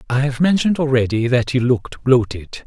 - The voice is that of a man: Yes, male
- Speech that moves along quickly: No, average, 180 wpm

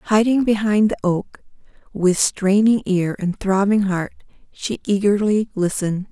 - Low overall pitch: No, high, 200 Hz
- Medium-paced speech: No, slow, 130 wpm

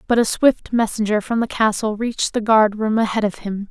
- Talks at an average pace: No, fast, 225 wpm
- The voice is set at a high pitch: Yes, high, 215 Hz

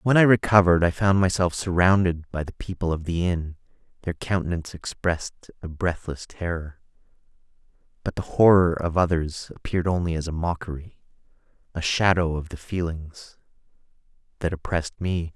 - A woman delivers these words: No, male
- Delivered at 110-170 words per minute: Yes, average, 145 wpm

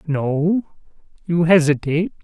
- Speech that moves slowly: Yes, slow, 80 wpm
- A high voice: No, medium, 165 Hz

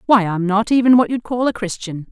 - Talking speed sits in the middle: No, fast, 255 wpm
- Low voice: No, high, 215 Hz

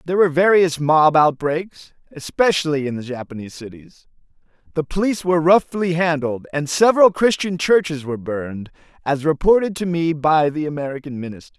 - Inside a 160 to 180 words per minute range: No, average, 150 wpm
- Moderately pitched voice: Yes, medium, 160 Hz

